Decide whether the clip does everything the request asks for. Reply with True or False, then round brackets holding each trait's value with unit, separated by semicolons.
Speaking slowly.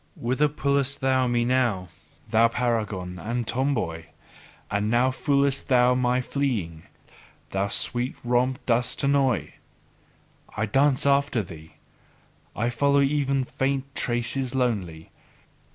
True (115 wpm)